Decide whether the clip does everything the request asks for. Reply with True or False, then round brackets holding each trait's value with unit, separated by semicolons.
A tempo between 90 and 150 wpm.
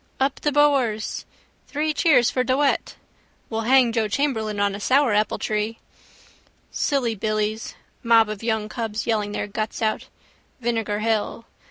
True (145 wpm)